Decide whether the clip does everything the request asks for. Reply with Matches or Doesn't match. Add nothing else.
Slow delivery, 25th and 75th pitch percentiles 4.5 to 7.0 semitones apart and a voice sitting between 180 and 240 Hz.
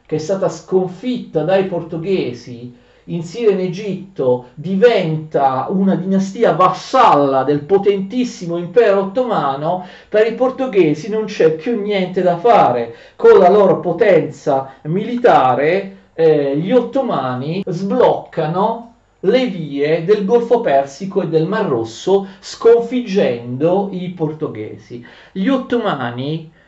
Matches